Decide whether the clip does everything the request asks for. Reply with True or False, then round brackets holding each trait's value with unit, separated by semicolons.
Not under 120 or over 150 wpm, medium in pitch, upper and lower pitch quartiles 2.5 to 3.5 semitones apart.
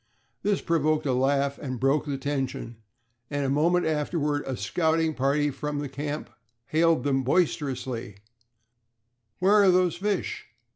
True (140 wpm; 145 Hz; 3.2 semitones)